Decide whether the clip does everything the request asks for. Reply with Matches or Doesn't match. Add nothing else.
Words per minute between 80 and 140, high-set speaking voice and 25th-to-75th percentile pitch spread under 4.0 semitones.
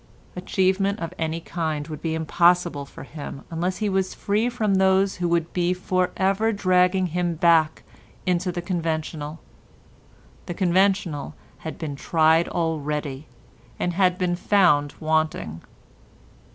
Doesn't match